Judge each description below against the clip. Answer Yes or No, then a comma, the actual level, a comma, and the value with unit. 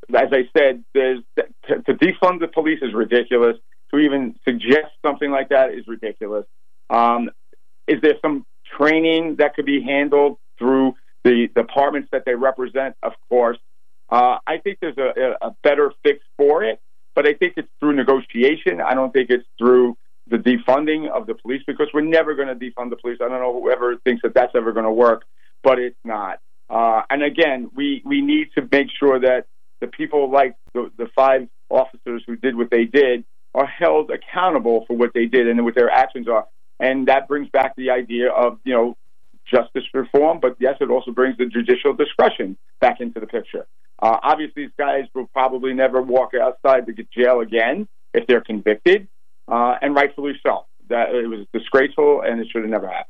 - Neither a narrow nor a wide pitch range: Yes, average, 3.8 semitones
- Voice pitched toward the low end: Yes, low, 130 Hz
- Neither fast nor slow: Yes, average, 195 wpm